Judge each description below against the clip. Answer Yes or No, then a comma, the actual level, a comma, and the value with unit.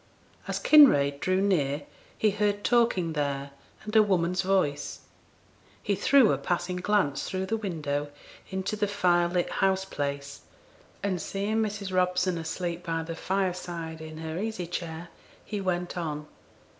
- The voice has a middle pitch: Yes, medium, 180 Hz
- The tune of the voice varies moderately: Yes, average, 3.7 semitones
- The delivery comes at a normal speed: Yes, average, 145 wpm